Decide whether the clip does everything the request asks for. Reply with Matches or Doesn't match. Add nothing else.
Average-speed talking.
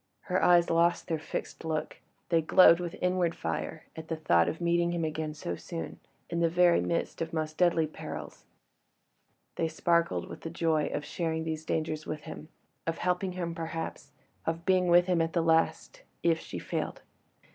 Matches